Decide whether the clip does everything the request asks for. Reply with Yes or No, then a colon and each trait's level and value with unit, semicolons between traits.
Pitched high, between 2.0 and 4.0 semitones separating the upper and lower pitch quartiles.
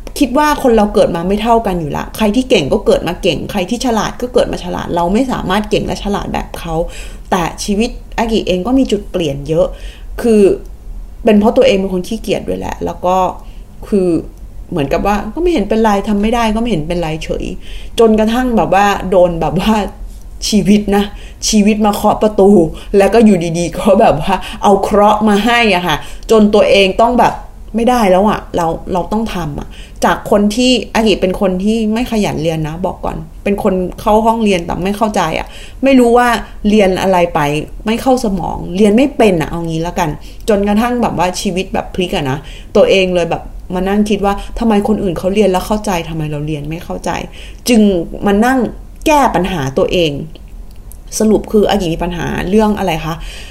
Yes: high, 200 Hz; average, 3.6 semitones